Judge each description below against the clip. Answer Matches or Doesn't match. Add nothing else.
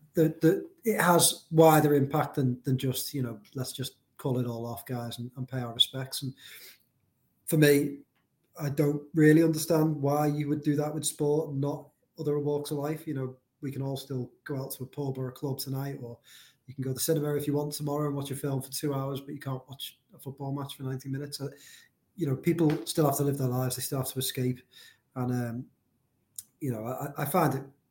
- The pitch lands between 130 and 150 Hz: Matches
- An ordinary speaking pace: Doesn't match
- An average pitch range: Doesn't match